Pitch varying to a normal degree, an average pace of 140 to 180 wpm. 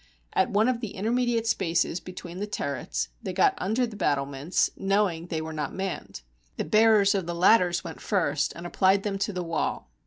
No: average, 4.0 semitones; average, 190 wpm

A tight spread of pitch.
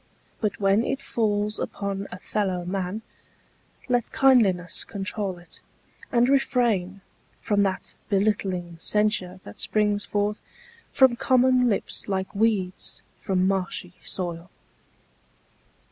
No: average, 3.0 semitones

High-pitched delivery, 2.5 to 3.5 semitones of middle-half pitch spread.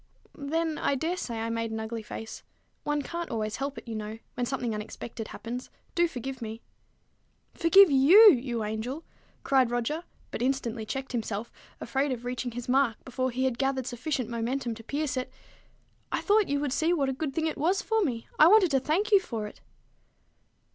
No: very high, 260 Hz; average, 4.6 semitones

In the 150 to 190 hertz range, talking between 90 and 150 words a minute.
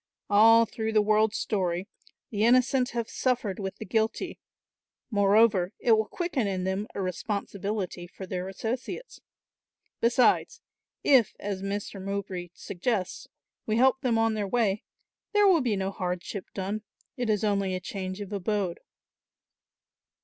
No: high, 205 Hz; average, 140 wpm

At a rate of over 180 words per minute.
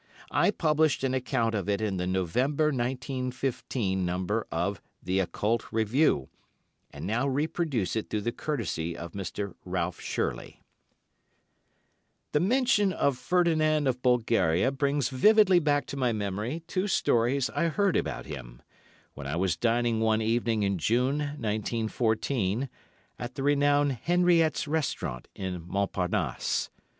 No: slow, 135 wpm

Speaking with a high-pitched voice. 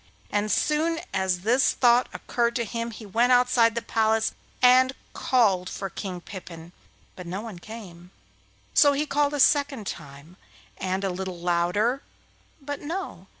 Yes: high, 220 Hz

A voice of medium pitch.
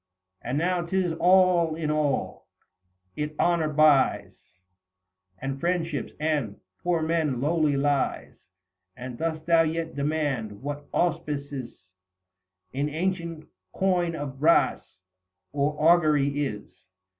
Yes: medium, 155 Hz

